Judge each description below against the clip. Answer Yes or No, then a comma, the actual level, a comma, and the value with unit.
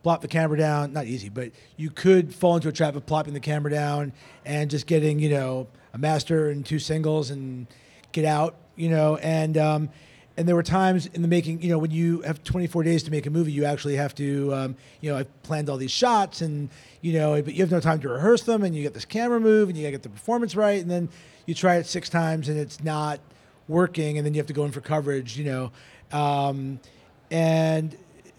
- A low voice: No, medium, 155 Hz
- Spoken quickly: Yes, fast, 240 wpm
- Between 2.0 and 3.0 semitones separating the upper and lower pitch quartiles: Yes, narrow, 2.5 semitones